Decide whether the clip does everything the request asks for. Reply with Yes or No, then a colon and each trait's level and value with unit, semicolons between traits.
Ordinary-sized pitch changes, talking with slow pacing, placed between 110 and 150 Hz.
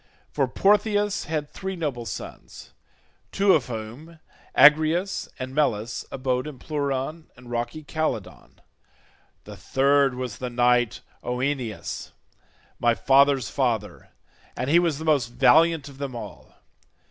Yes: average, 4.2 semitones; slow, 125 wpm; medium, 140 Hz